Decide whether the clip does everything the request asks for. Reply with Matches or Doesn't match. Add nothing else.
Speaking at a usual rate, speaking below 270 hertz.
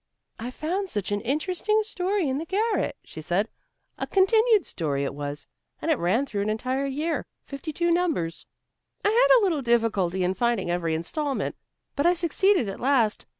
Doesn't match